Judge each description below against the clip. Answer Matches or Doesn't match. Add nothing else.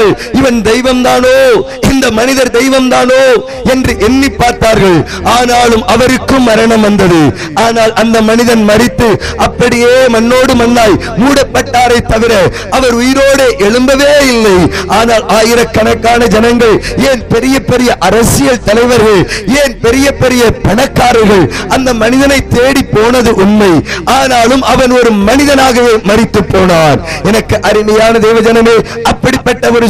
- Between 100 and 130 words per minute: Matches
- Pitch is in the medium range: Doesn't match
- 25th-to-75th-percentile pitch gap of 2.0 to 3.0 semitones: Matches